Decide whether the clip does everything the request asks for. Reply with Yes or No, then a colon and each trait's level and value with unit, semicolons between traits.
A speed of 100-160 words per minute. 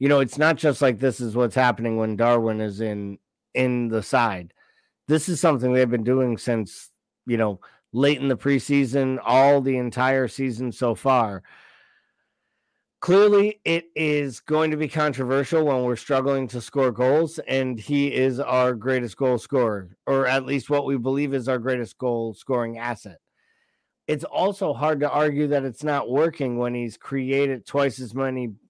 No: average, 175 wpm